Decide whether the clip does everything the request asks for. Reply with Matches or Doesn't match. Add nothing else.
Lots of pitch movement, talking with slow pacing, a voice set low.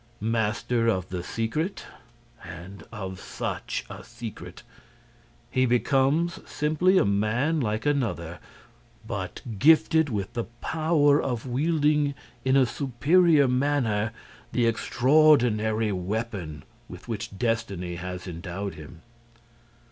Matches